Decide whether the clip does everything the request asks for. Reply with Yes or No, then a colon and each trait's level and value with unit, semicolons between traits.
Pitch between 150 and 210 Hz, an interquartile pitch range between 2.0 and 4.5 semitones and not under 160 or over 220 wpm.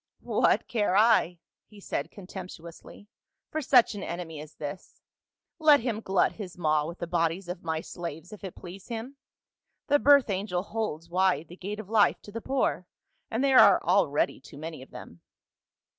No: medium, 185 Hz; average, 4.9 semitones; average, 175 wpm